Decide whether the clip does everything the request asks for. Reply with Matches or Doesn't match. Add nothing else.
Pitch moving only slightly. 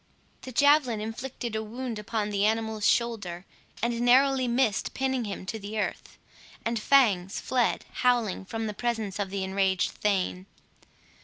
Doesn't match